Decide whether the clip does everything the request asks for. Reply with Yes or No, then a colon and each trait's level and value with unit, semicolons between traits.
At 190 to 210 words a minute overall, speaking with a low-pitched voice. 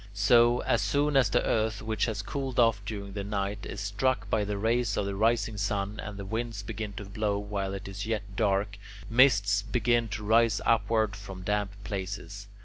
Yes: average, 195 wpm; low, 105 Hz